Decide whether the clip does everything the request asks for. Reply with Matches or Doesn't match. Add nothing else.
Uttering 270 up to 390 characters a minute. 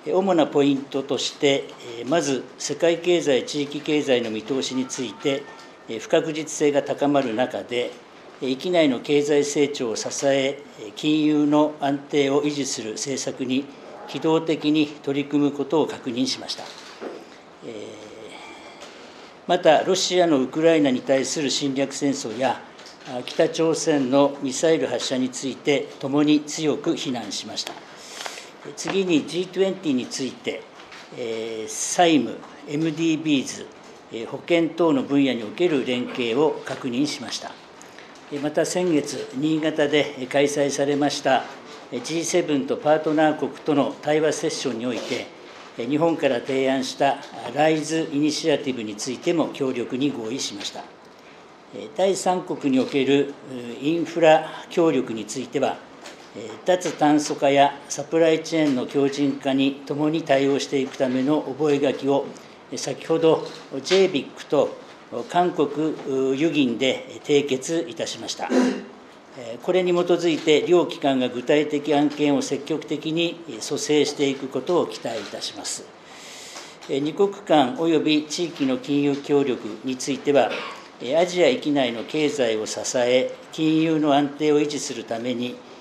Doesn't match